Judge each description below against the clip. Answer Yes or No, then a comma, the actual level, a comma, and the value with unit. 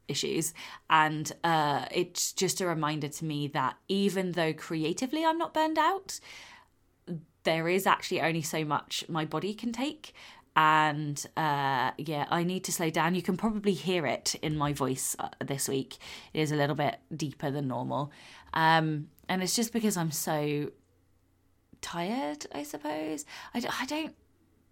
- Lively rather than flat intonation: No, average, 4.3 semitones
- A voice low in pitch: No, medium, 160 Hz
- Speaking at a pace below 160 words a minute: No, average, 165 wpm